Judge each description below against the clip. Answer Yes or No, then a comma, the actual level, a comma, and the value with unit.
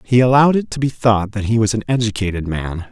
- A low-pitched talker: Yes, low, 110 Hz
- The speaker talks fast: Yes, fast, 245 wpm